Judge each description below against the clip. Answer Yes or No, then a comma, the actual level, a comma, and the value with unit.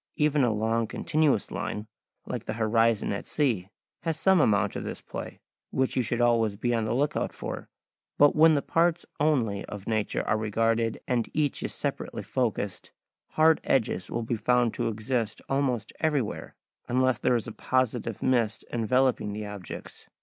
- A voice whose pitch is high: No, low, 120 Hz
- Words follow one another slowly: No, average, 170 wpm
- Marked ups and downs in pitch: No, average, 3.7 semitones